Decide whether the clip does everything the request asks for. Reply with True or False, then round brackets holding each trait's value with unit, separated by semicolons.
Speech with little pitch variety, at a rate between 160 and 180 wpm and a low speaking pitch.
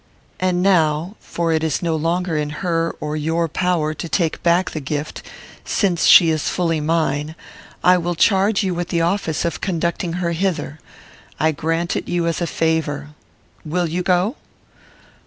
False (2.1 semitones; 170 wpm; 170 Hz)